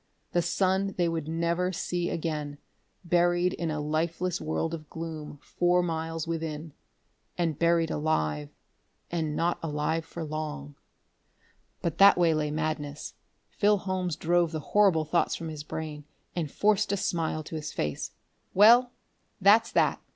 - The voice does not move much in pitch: Yes, narrow, 2.2 semitones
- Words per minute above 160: No, average, 145 wpm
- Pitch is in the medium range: Yes, medium, 165 Hz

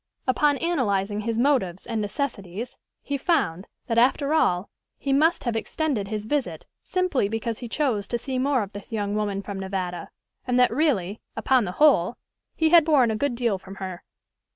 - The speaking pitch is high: Yes, high, 230 Hz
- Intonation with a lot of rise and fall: Yes, wide, 5.9 semitones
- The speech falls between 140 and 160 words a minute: No, average, 180 wpm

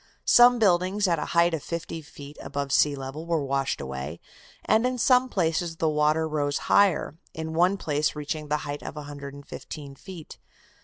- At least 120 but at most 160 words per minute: No, average, 170 wpm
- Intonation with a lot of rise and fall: No, average, 3.3 semitones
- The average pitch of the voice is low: No, medium, 155 Hz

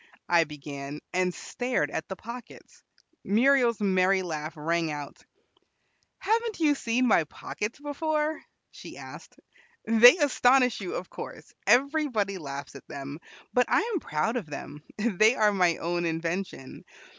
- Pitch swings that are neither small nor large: No, wide, 7.6 semitones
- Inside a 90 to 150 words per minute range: Yes, average, 140 wpm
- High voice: Yes, high, 200 Hz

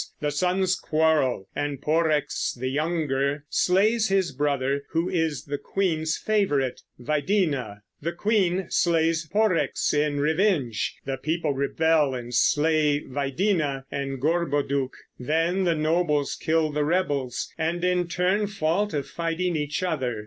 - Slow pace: Yes, slow, 130 wpm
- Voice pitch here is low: No, medium, 155 Hz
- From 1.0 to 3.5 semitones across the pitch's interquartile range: No, average, 3.9 semitones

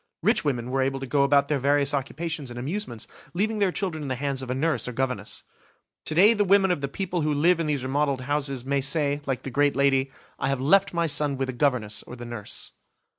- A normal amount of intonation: Yes, average, 3.1 semitones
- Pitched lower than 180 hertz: Yes, medium, 140 Hz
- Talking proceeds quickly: Yes, fast, 245 wpm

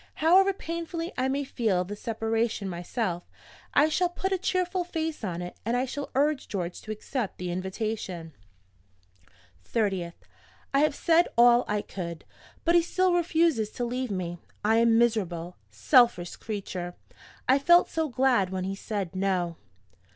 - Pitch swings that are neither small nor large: No, wide, 8.5 semitones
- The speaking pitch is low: No, high, 230 Hz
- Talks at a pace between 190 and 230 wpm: No, average, 160 wpm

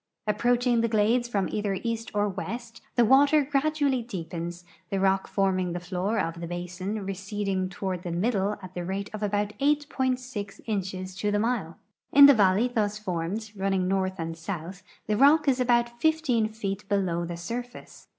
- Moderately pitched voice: No, high, 205 Hz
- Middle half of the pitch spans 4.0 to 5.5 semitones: Yes, average, 4.3 semitones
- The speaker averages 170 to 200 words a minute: Yes, average, 175 wpm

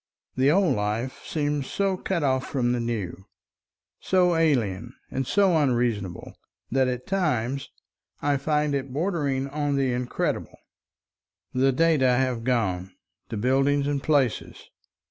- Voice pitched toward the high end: No, low, 135 Hz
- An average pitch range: Yes, average, 3.5 semitones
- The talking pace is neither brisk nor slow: No, slow, 130 wpm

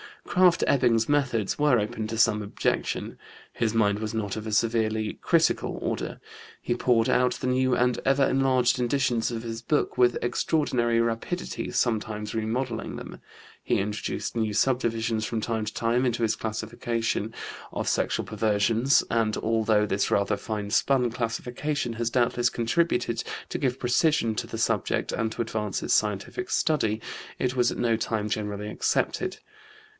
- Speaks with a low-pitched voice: Yes, low, 115 Hz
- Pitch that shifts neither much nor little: No, narrow, 2.3 semitones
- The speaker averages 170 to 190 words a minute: No, average, 155 wpm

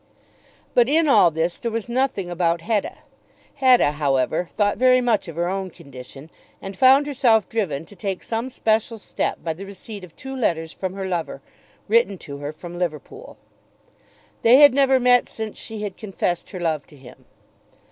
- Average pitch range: No, wide, 6.3 semitones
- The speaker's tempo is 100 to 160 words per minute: No, average, 180 wpm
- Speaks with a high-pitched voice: Yes, high, 195 Hz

